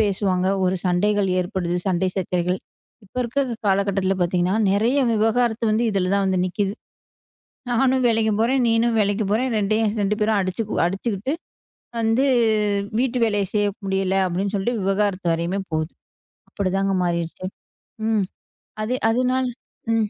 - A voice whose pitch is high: Yes, high, 200 Hz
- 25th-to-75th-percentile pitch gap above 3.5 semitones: No, average, 3.2 semitones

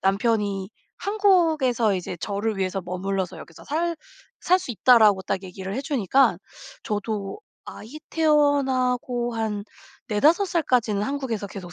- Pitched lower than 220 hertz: No, high, 225 Hz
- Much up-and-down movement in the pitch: Yes, wide, 6.4 semitones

